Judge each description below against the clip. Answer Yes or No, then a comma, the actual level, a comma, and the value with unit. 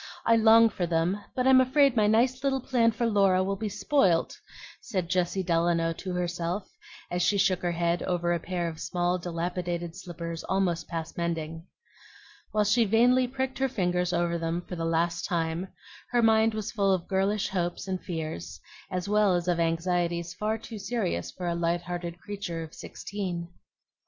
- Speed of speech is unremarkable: Yes, average, 180 wpm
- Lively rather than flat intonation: No, average, 3.7 semitones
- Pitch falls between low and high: Yes, medium, 180 Hz